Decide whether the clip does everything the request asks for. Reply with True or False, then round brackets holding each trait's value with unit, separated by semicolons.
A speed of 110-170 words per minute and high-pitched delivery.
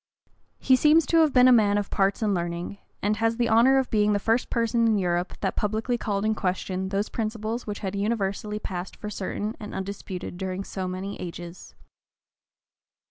False (190 wpm; 205 Hz)